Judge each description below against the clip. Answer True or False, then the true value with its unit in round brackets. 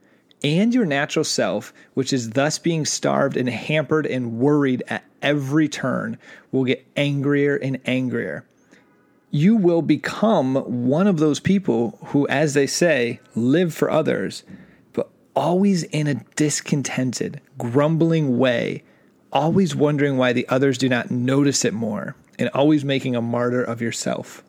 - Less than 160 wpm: True (145 wpm)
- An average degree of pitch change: True (3.4 semitones)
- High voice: False (140 Hz)